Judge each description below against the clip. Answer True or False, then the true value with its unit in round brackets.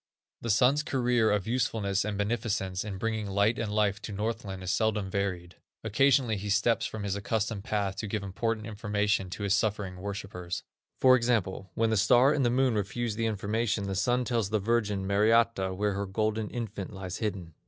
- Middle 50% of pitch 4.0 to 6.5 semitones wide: False (2.5 semitones)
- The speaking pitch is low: True (105 Hz)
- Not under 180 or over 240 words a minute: True (185 wpm)